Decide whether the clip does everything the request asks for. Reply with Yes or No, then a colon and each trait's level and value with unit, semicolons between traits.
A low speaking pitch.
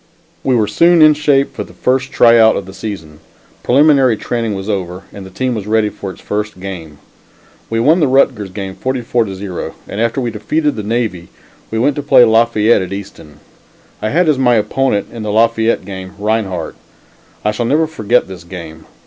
Yes: low, 110 Hz